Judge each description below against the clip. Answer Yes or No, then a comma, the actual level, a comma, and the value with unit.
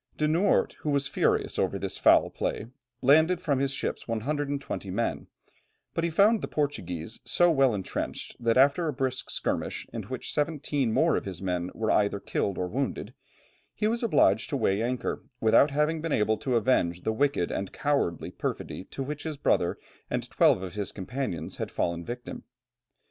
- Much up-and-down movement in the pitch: Yes, wide, 6.4 semitones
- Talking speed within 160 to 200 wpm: Yes, average, 180 wpm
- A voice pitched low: Yes, low, 130 Hz